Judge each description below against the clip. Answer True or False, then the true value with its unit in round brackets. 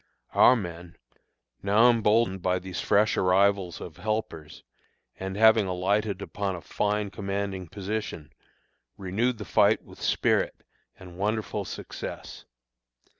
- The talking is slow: True (120 wpm)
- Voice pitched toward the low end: True (100 Hz)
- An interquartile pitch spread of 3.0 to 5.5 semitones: False (2.6 semitones)